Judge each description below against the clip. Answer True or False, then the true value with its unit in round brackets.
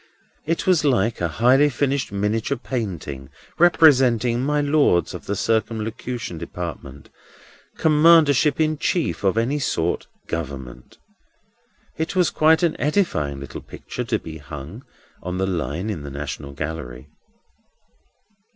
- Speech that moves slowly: True (125 wpm)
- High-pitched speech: False (110 Hz)